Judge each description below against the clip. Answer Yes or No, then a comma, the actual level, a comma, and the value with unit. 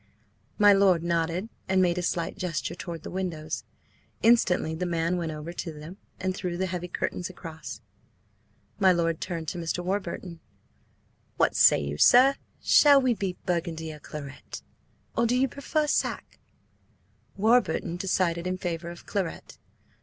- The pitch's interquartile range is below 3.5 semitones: Yes, narrow, 2.5 semitones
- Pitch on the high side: No, medium, 180 Hz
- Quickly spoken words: No, average, 155 wpm